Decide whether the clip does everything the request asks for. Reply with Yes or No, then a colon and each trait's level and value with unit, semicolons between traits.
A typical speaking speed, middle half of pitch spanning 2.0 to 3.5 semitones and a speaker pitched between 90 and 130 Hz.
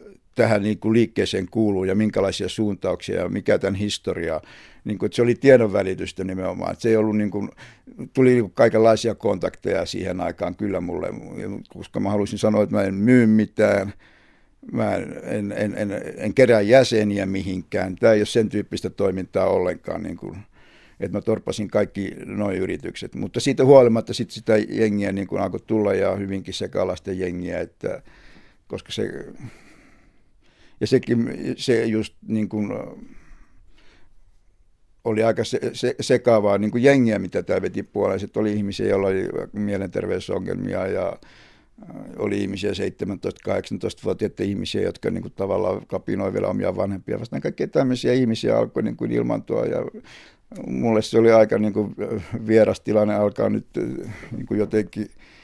Yes: average, 135 wpm; narrow, 2.4 semitones; low, 105 Hz